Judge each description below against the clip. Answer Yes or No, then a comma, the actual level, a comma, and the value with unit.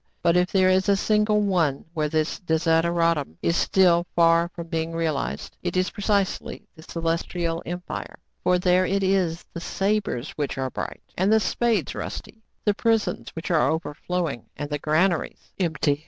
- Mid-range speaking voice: Yes, medium, 170 Hz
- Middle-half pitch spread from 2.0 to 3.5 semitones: Yes, average, 2.8 semitones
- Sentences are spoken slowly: No, average, 165 wpm